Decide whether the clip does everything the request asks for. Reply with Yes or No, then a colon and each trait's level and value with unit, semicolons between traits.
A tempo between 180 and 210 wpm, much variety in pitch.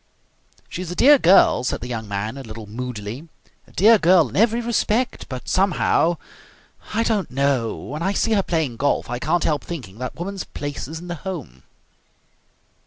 Yes: average, 185 wpm; wide, 7.4 semitones